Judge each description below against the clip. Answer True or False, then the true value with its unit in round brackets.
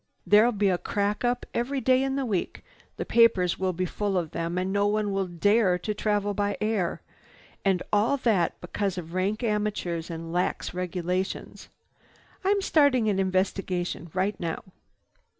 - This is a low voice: False (200 Hz)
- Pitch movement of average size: True (3.0 semitones)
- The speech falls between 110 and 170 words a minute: True (165 wpm)